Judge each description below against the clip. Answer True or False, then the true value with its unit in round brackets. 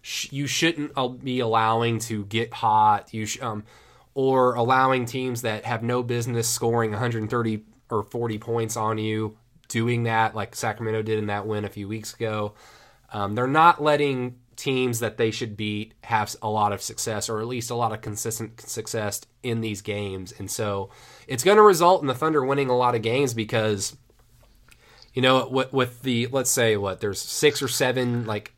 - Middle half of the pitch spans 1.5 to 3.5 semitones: True (2.7 semitones)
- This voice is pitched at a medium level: False (115 Hz)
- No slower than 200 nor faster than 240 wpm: False (185 wpm)